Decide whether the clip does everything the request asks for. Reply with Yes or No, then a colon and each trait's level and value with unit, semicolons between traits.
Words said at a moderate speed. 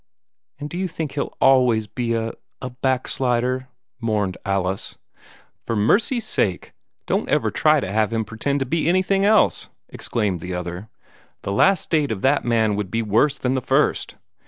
Yes: average, 175 wpm